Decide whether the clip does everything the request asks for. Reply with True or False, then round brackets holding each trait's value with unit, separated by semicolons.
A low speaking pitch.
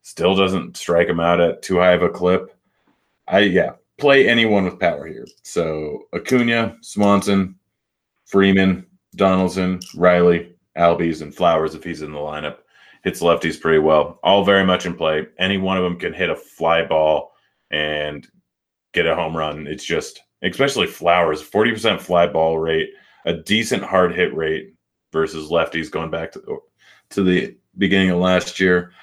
True (90 Hz)